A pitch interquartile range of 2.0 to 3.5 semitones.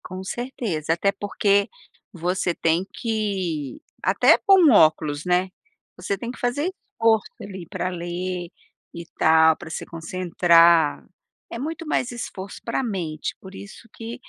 No: average, 4.9 semitones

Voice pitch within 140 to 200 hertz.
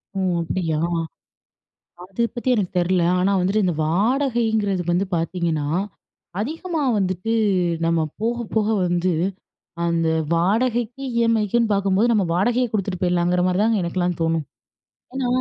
Yes: high, 195 Hz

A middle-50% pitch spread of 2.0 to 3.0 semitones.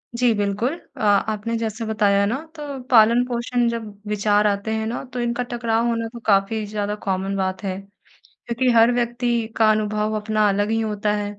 Yes: narrow, 2.4 semitones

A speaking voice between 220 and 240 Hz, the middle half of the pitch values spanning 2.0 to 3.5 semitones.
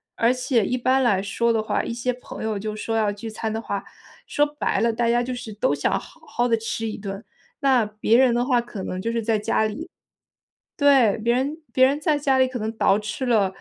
Yes: high, 230 Hz; average, 2.9 semitones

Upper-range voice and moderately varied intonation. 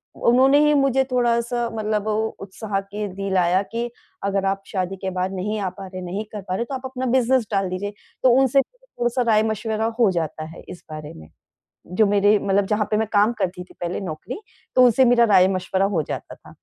Yes: high, 210 Hz; average, 4.0 semitones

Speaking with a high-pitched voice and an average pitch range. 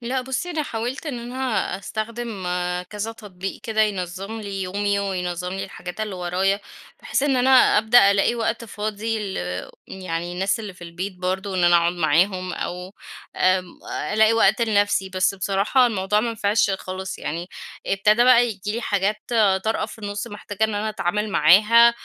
Yes: high, 205 Hz; average, 3.2 semitones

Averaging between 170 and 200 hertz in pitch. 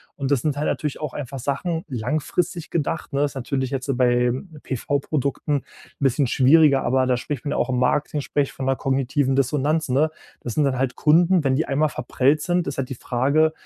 No: medium, 140 Hz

